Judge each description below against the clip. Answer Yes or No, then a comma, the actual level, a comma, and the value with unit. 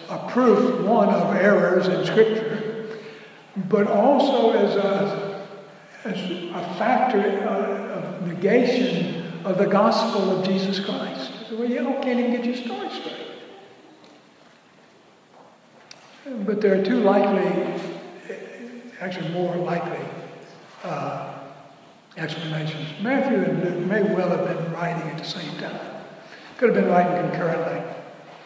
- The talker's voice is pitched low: No, high, 195 Hz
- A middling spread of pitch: Yes, average, 3.7 semitones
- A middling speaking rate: No, slow, 120 wpm